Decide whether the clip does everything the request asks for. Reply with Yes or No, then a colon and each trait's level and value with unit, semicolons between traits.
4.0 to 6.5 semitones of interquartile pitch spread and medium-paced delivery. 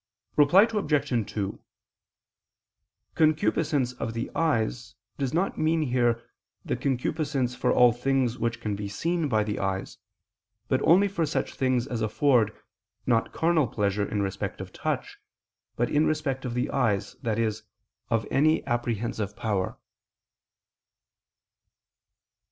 No: average, 5.0 semitones; slow, 130 wpm